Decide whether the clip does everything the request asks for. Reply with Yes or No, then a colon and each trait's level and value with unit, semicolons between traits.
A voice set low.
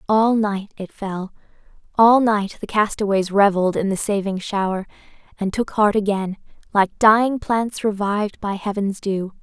No: high, 205 Hz